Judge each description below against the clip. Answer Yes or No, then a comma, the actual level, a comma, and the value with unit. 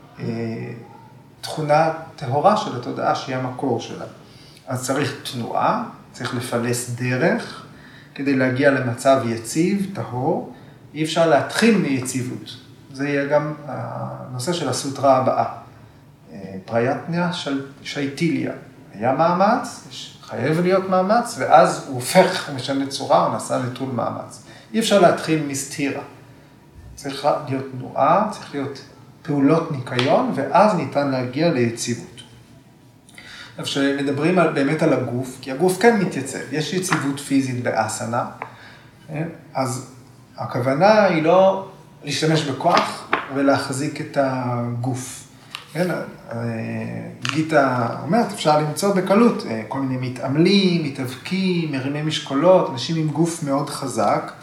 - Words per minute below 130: Yes, average, 110 wpm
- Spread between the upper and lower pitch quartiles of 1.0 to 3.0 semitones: No, average, 3.7 semitones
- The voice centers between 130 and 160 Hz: Yes, medium, 140 Hz